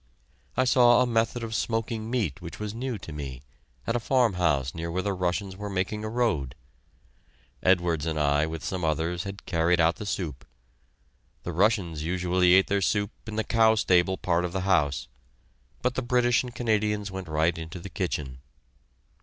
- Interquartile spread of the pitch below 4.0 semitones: No, average, 5.0 semitones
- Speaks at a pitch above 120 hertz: No, very low, 95 Hz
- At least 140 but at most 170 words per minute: No, average, 180 wpm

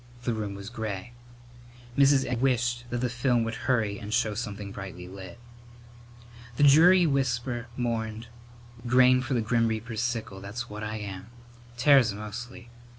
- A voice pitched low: Yes, low, 120 Hz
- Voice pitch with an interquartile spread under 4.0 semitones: Yes, average, 2.8 semitones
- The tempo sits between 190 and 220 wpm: No, average, 150 wpm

